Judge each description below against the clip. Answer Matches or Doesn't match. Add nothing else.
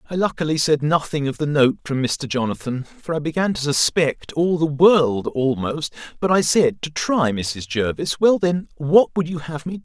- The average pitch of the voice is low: Doesn't match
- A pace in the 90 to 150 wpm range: Doesn't match